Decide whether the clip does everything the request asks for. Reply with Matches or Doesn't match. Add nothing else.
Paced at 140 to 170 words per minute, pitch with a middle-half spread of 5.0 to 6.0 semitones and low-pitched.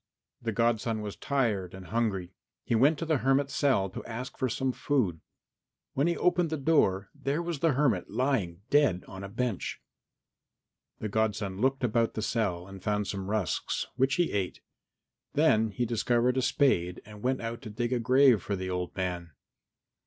Doesn't match